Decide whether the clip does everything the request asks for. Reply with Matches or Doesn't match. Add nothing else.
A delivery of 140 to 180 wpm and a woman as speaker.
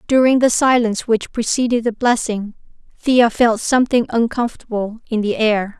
Matches